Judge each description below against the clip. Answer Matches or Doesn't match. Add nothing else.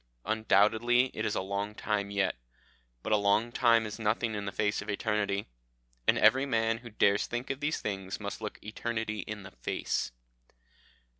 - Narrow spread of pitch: Matches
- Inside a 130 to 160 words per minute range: Doesn't match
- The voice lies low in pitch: Matches